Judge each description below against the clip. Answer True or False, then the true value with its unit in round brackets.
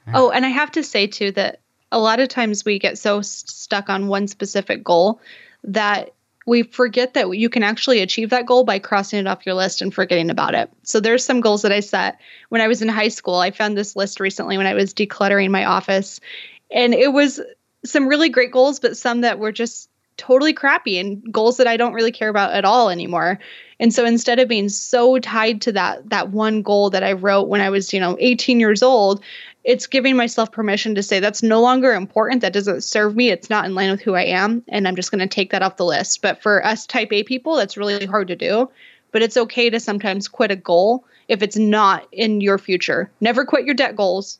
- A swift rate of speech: True (235 wpm)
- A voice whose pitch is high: True (215 Hz)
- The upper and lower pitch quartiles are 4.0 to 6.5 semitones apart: False (3.4 semitones)